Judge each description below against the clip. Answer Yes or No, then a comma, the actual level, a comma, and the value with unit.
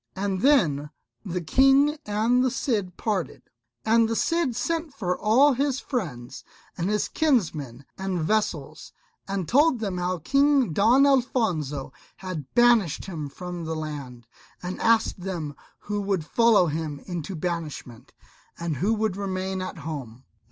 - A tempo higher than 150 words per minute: No, average, 145 wpm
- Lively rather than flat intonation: Yes, wide, 6.8 semitones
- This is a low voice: No, high, 190 Hz